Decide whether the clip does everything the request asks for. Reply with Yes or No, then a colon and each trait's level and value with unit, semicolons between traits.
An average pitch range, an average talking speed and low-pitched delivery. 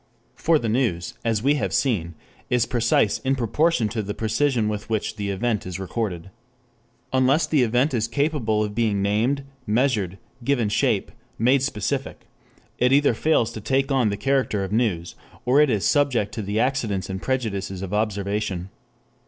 Yes: average, 4.4 semitones; average, 170 wpm; low, 115 Hz